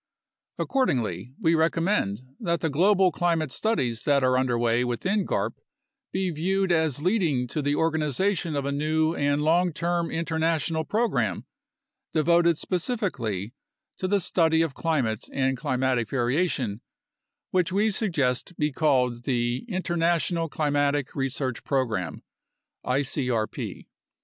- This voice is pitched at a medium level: Yes, medium, 155 Hz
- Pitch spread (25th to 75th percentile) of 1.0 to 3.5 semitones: No, average, 5.1 semitones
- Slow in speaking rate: Yes, slow, 125 wpm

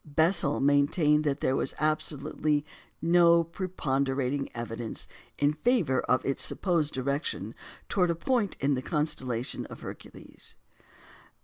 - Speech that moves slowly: Yes, slow, 115 wpm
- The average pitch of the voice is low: No, medium, 150 Hz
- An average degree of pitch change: Yes, average, 3.6 semitones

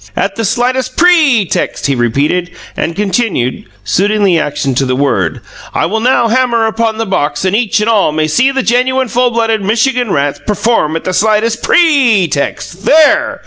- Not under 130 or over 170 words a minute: No, average, 185 wpm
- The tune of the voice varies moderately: No, wide, 6.9 semitones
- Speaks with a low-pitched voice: No, high, 215 Hz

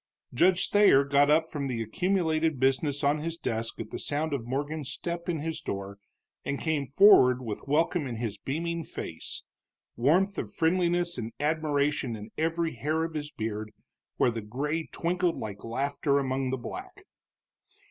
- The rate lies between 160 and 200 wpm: Yes, average, 165 wpm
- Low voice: No, medium, 145 Hz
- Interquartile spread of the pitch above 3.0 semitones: Yes, average, 4.7 semitones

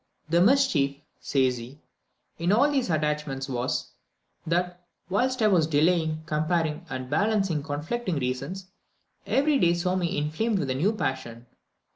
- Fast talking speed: No, average, 140 wpm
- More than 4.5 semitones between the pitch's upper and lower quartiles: Yes, average, 5.2 semitones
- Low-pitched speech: No, medium, 165 Hz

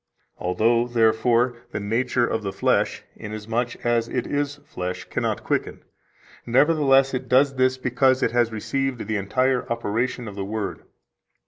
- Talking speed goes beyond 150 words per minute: No, average, 145 wpm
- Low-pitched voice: Yes, low, 120 Hz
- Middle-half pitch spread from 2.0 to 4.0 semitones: Yes, average, 2.7 semitones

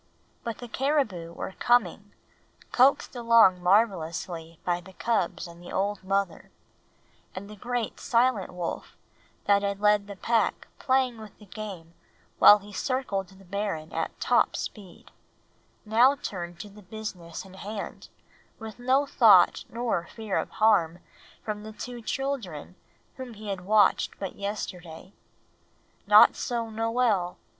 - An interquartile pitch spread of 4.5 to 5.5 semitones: No, average, 3.9 semitones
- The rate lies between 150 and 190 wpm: No, average, 140 wpm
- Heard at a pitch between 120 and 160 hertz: No, high, 205 Hz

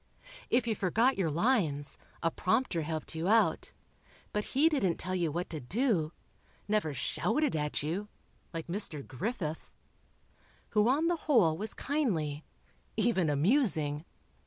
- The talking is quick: No, slow, 135 wpm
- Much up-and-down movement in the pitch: Yes, wide, 7.0 semitones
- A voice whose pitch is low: No, medium, 185 Hz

